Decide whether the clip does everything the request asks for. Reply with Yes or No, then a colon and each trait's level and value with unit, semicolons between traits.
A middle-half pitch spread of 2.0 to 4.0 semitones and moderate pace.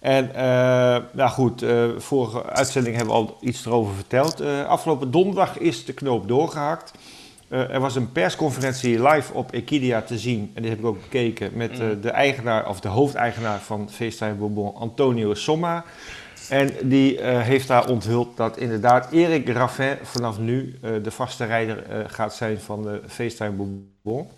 Yes: average, 3.1 semitones; average, 175 wpm